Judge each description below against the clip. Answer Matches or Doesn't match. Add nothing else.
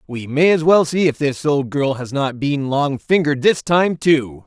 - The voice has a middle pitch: Matches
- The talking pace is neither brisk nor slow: Doesn't match